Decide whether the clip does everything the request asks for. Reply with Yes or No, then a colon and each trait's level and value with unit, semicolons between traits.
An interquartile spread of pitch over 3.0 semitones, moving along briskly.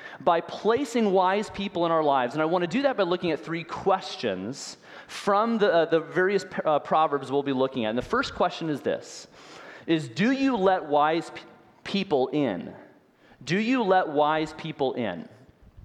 No: average, 4.6 semitones; average, 185 wpm